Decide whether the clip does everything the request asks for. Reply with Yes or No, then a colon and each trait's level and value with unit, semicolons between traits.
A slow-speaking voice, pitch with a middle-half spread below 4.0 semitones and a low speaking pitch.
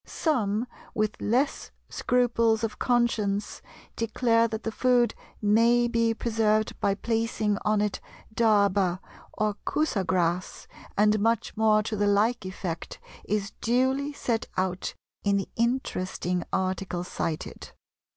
No: slow, 120 wpm; average, 2.7 semitones; high, 215 Hz